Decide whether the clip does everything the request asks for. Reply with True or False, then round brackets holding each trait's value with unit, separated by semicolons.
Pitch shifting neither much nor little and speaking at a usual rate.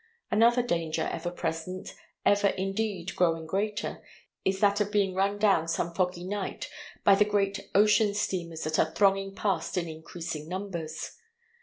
True (3.3 semitones; 150 wpm)